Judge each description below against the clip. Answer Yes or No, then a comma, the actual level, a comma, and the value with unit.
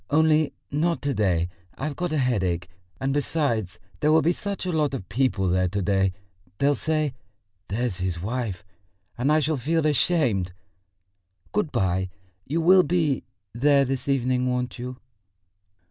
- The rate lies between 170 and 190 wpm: No, average, 155 wpm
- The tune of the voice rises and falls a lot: Yes, wide, 7.0 semitones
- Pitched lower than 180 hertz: Yes, low, 135 Hz